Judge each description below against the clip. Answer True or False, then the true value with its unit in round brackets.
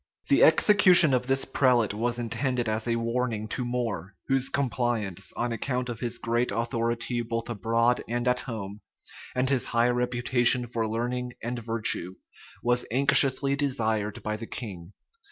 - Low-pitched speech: True (120 Hz)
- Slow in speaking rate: False (155 wpm)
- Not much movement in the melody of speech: True (1.7 semitones)